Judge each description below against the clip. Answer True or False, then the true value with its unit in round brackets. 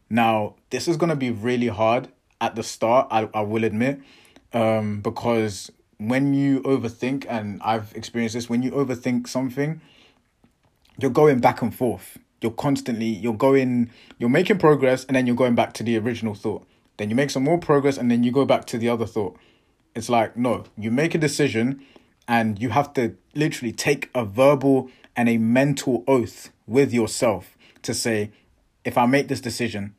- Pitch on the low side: True (120 Hz)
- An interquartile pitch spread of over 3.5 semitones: False (3.2 semitones)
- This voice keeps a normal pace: True (185 wpm)